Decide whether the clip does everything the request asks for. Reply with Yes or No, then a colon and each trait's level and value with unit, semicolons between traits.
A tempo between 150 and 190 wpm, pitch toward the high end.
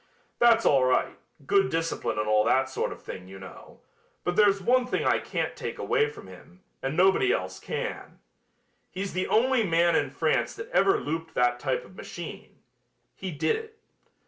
No: average, 180 wpm; medium, 175 Hz